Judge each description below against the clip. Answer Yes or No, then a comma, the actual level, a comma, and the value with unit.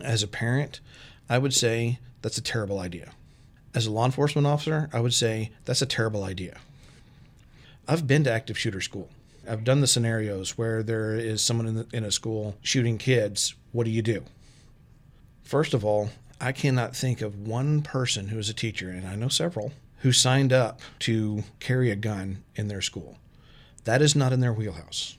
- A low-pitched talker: Yes, low, 115 Hz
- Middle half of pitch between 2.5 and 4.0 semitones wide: Yes, average, 3.2 semitones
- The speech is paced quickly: No, average, 190 wpm